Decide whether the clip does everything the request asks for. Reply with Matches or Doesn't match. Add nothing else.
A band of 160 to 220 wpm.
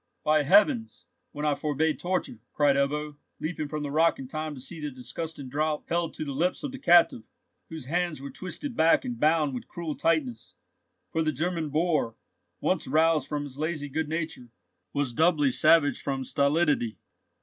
Matches